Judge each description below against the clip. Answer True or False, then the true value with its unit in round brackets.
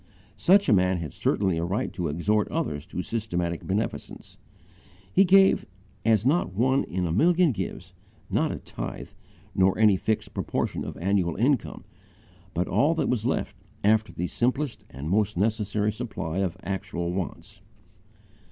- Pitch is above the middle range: False (105 Hz)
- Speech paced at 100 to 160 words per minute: True (150 wpm)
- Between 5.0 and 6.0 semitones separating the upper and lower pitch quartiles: True (5.3 semitones)